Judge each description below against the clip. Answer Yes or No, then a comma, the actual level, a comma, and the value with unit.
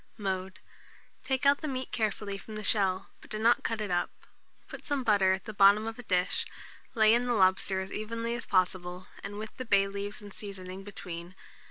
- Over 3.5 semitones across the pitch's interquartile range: No, average, 3.0 semitones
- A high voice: Yes, high, 205 Hz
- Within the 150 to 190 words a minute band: No, average, 200 wpm